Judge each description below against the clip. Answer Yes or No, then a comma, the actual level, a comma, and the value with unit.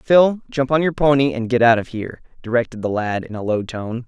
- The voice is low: Yes, low, 125 Hz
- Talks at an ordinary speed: No, fast, 250 wpm